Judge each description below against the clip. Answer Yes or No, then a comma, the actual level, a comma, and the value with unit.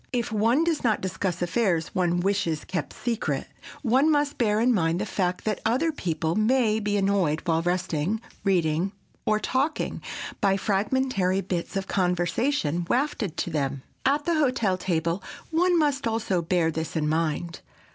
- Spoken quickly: No, average, 155 wpm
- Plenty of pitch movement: Yes, wide, 5.7 semitones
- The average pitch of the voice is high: Yes, high, 195 Hz